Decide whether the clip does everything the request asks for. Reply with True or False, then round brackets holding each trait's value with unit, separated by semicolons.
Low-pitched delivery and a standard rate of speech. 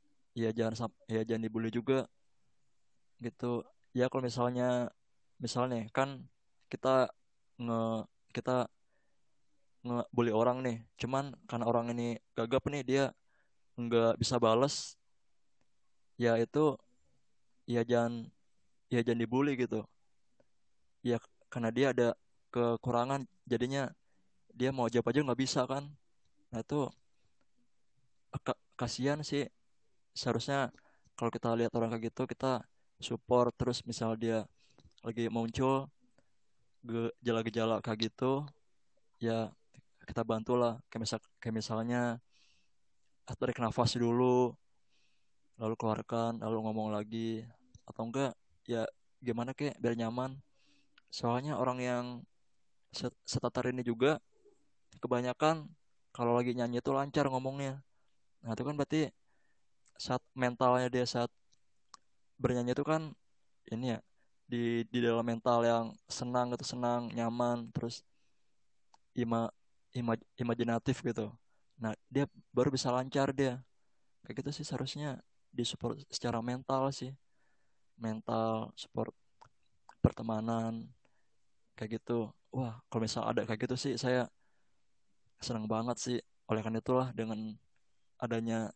True (120 Hz; 115 wpm)